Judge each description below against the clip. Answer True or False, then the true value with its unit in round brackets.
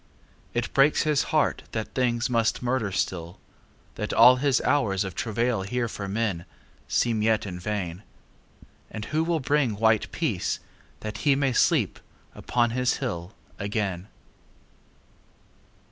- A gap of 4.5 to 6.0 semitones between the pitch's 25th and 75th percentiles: False (4.1 semitones)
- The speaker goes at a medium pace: False (125 wpm)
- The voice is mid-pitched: False (115 Hz)